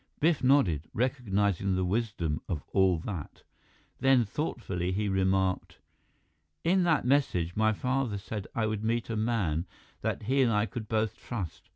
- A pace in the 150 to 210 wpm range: Yes, average, 155 wpm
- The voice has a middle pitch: No, low, 105 Hz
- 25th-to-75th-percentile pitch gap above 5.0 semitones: No, average, 4.6 semitones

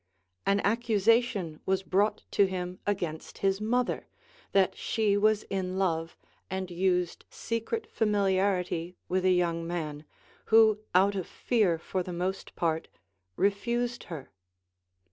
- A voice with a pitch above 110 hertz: Yes, high, 190 Hz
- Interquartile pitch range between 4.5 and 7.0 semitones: No, average, 2.9 semitones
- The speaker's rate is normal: No, slow, 130 wpm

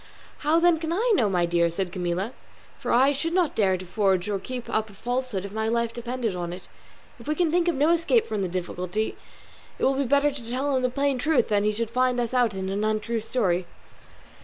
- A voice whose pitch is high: Yes, high, 235 Hz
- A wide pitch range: Yes, wide, 6.2 semitones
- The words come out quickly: Yes, fast, 240 wpm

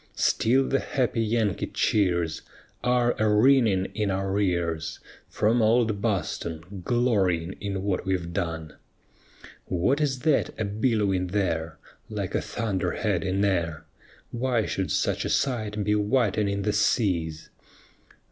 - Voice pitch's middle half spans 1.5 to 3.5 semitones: No, average, 4.0 semitones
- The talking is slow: Yes, slow, 130 wpm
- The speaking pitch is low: Yes, low, 100 Hz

